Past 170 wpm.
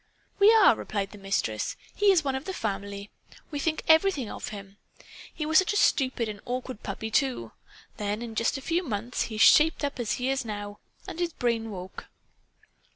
Yes: average, 195 wpm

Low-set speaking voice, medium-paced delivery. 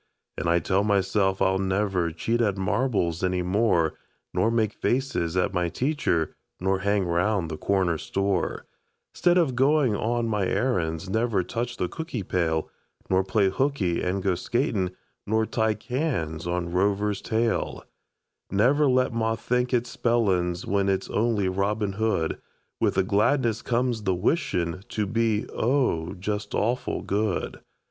Yes: low, 100 Hz; average, 150 wpm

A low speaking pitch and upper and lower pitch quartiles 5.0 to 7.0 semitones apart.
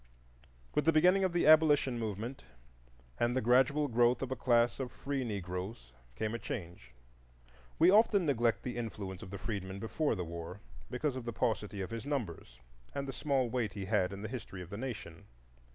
Yes: low, 120 Hz; wide, 5.5 semitones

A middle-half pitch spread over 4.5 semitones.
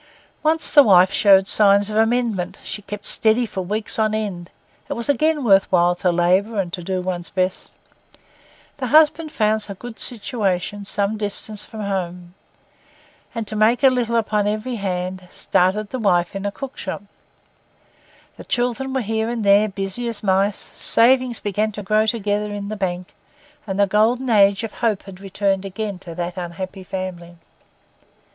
No: average, 3.0 semitones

